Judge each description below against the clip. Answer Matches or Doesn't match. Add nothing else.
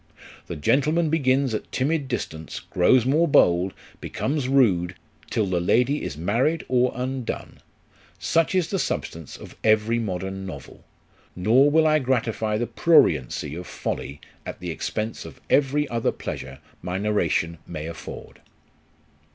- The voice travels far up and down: Matches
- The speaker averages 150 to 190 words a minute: Doesn't match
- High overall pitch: Doesn't match